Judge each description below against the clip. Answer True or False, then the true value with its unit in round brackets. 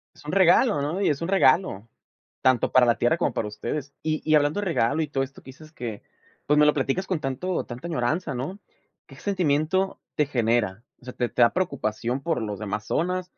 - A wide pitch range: True (5.9 semitones)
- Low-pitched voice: False (145 Hz)